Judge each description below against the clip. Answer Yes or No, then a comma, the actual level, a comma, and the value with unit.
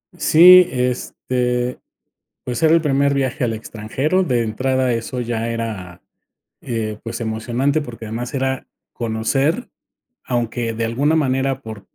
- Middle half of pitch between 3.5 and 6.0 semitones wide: No, average, 3.1 semitones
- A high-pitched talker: No, low, 125 Hz